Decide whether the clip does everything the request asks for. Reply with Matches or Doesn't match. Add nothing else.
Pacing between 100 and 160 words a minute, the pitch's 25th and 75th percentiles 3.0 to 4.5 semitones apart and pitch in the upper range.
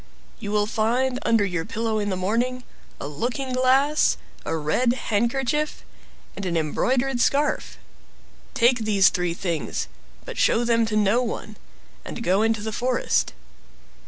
Matches